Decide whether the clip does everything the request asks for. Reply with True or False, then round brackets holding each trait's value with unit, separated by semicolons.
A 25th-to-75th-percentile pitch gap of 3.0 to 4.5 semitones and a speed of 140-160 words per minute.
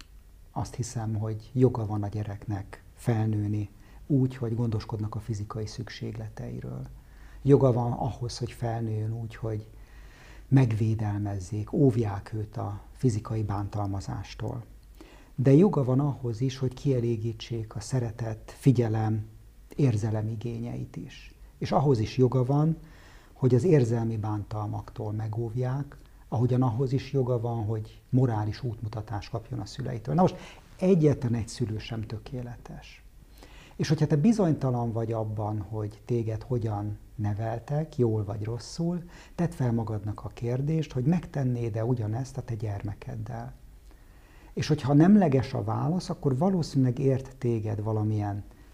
False (3.4 semitones; 125 wpm)